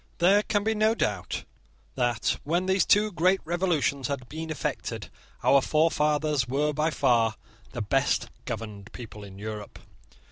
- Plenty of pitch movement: Yes, wide, 6.8 semitones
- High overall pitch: No, medium, 150 Hz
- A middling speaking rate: Yes, average, 145 wpm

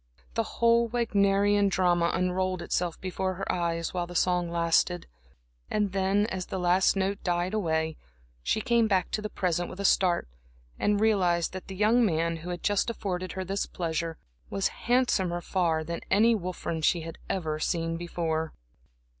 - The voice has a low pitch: No, medium, 185 Hz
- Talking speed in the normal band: Yes, average, 170 wpm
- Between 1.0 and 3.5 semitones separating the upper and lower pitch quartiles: Yes, average, 2.8 semitones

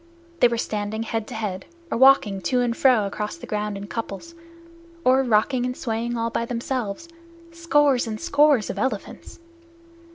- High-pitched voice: Yes, high, 235 Hz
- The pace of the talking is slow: No, average, 165 wpm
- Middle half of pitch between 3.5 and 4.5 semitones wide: Yes, average, 3.8 semitones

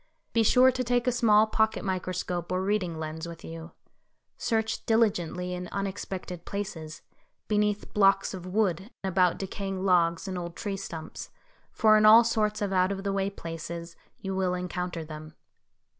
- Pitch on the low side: No, high, 190 Hz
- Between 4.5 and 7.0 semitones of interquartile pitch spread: No, average, 3.3 semitones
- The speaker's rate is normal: Yes, average, 160 wpm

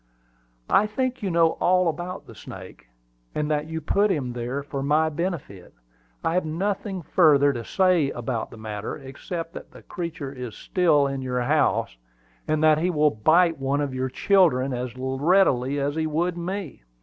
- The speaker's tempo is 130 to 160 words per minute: No, average, 175 wpm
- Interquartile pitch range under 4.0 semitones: No, average, 4.9 semitones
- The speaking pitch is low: No, medium, 150 Hz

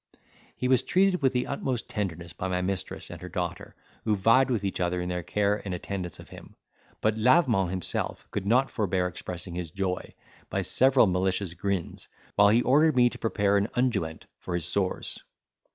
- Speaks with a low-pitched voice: Yes, low, 100 Hz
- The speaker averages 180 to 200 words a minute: Yes, average, 185 wpm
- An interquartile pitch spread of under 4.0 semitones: No, average, 5.1 semitones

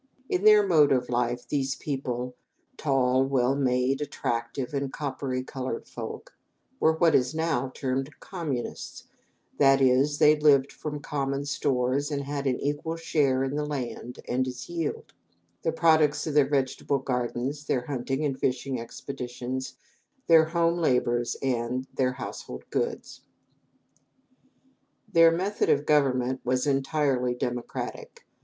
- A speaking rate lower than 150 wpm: Yes, slow, 135 wpm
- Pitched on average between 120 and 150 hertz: Yes, low, 135 Hz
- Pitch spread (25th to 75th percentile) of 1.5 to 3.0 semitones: Yes, average, 2.7 semitones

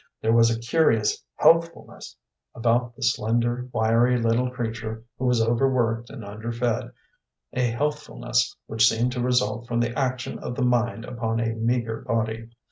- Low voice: Yes, low, 120 Hz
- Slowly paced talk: No, average, 155 wpm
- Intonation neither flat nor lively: No, narrow, 1.6 semitones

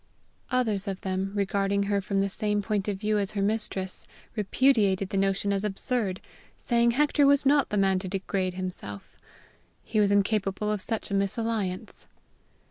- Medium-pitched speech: No, high, 200 Hz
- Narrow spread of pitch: Yes, narrow, 2.0 semitones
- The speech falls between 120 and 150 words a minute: No, average, 165 wpm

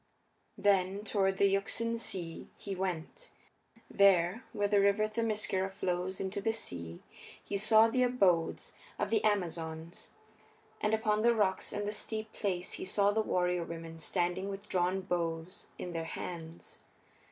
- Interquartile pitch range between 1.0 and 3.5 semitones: Yes, average, 3.2 semitones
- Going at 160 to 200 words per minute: No, average, 150 wpm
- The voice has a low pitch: No, high, 195 Hz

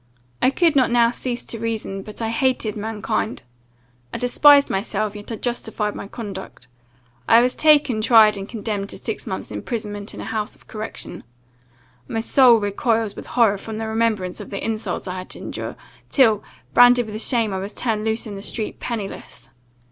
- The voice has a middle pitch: No, high, 220 Hz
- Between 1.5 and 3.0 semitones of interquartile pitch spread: Yes, narrow, 2.4 semitones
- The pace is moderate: Yes, average, 185 wpm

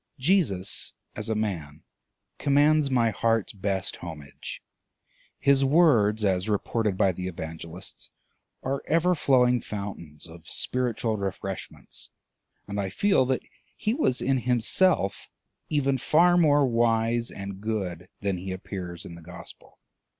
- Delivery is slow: Yes, slow, 130 wpm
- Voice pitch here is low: Yes, low, 110 Hz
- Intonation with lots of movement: Yes, wide, 6.1 semitones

